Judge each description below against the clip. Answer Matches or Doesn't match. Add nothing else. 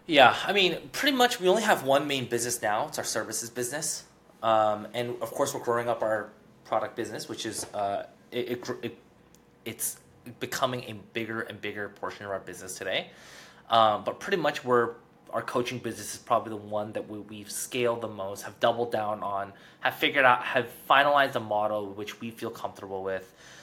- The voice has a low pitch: Matches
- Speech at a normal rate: Matches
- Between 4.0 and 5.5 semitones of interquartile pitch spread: Doesn't match